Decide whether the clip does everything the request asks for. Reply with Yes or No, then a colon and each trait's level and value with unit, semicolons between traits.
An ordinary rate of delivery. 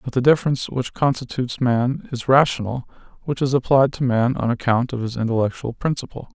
Yes: average, 180 wpm